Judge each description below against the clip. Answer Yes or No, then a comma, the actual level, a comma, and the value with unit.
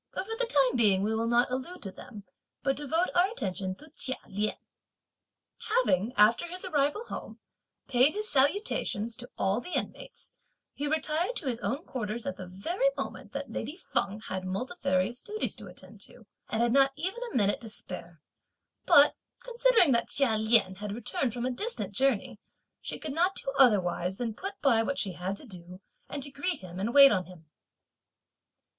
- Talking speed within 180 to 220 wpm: Yes, average, 185 wpm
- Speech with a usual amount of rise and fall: No, wide, 7.0 semitones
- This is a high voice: Yes, high, 245 Hz